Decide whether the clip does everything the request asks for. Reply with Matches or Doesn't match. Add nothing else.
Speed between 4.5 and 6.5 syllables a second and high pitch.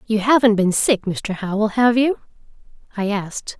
Matches